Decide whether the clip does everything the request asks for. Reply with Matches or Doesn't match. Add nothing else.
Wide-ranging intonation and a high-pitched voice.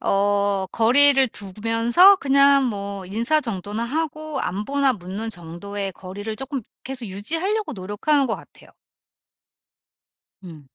Matches